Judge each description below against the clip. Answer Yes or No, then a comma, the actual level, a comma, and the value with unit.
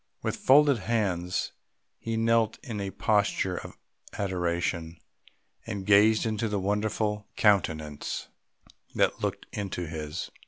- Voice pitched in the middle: No, low, 100 Hz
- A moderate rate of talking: No, slow, 115 wpm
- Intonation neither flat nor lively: Yes, average, 3.7 semitones